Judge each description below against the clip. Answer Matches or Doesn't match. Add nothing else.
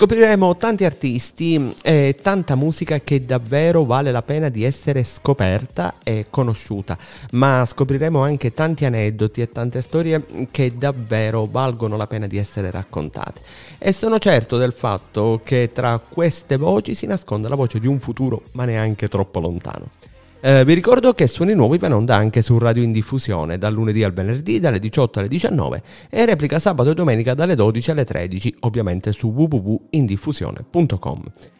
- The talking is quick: Doesn't match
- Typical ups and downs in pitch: Doesn't match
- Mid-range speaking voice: Doesn't match